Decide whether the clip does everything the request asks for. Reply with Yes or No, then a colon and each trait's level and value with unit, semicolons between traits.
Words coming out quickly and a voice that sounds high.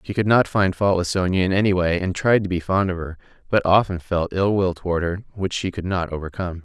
No: fast, 260 wpm; very low, 90 Hz